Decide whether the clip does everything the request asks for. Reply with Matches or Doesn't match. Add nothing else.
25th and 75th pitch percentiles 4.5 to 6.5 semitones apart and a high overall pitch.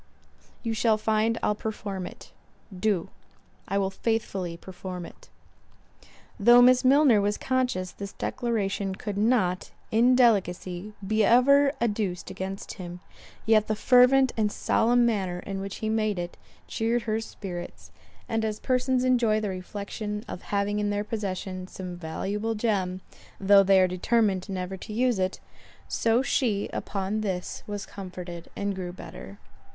Doesn't match